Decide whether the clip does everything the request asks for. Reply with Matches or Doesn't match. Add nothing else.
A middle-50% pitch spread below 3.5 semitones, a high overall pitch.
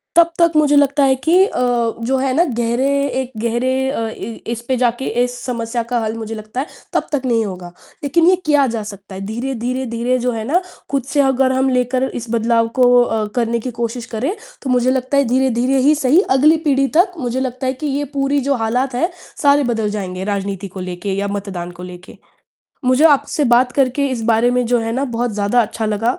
Matches